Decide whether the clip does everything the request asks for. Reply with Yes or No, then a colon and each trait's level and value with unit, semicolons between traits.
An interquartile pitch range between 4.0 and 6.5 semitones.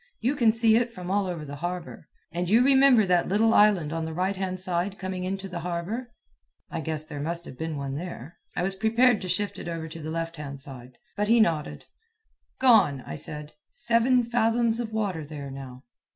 Yes: wide, 5.6 semitones